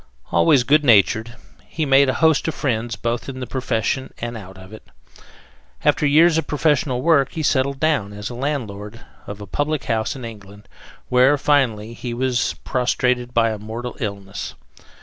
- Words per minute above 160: Yes, average, 170 wpm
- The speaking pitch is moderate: No, low, 125 Hz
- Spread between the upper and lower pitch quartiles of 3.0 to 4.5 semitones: Yes, average, 4.2 semitones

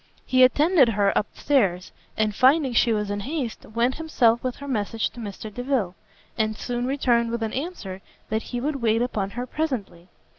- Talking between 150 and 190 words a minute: Yes, average, 185 wpm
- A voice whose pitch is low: No, high, 235 Hz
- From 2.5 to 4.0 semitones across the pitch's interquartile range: Yes, average, 3.7 semitones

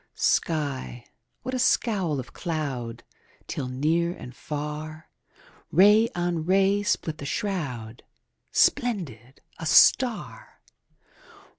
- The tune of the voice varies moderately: No, wide, 6.4 semitones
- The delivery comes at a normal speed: No, slow, 105 wpm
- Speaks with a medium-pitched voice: Yes, medium, 160 Hz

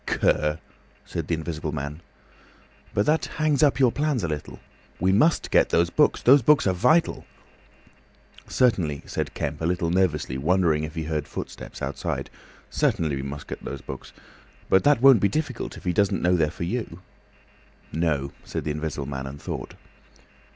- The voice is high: No, very low, 85 Hz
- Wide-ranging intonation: Yes, wide, 7.8 semitones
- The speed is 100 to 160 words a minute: No, average, 170 wpm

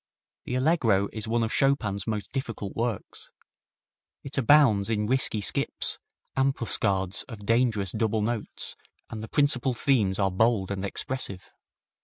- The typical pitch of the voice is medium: No, low, 110 Hz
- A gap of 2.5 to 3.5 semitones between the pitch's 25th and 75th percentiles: No, average, 4.1 semitones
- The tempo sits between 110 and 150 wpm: Yes, slow, 135 wpm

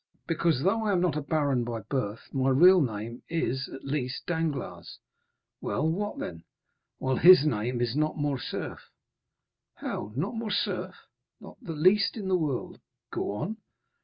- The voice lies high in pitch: No, medium, 145 Hz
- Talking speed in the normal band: Yes, average, 150 wpm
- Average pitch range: No, wide, 5.9 semitones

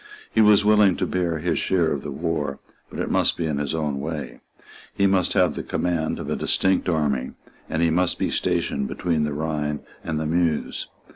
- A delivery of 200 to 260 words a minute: Yes, fast, 205 wpm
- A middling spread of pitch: Yes, average, 3.0 semitones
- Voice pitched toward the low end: Yes, very low, 80 Hz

